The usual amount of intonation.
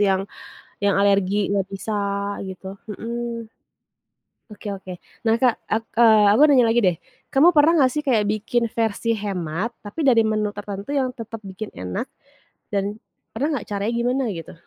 Yes: average, 3.1 semitones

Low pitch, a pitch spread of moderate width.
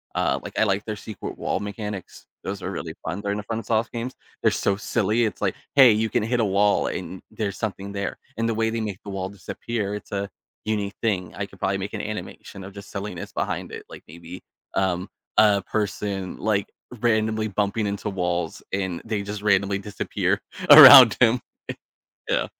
No: low, 105 Hz; narrow, 2.0 semitones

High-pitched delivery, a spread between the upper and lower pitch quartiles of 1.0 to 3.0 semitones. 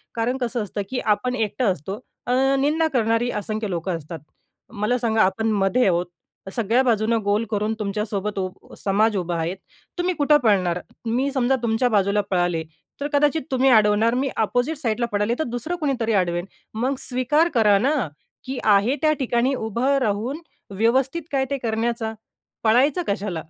No: high, 225 Hz; average, 4.1 semitones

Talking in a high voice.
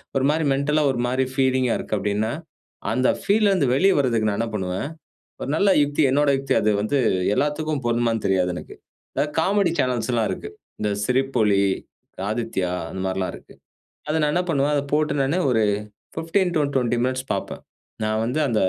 No: low, 130 Hz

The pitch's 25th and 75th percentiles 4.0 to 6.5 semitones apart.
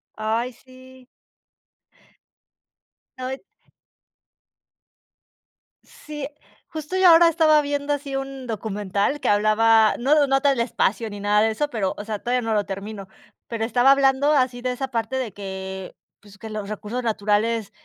Yes: average, 4.4 semitones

